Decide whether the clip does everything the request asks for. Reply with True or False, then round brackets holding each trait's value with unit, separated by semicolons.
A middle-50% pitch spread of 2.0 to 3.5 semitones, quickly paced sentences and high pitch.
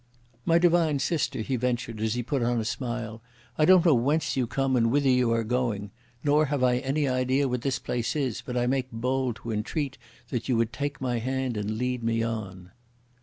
False (2.9 semitones; 215 wpm; 125 Hz)